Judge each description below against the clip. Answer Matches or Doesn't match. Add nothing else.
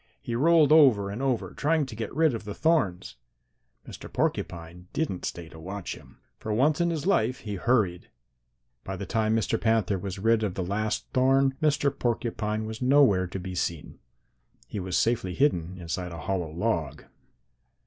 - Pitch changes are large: Matches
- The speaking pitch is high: Doesn't match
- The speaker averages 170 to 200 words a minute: Matches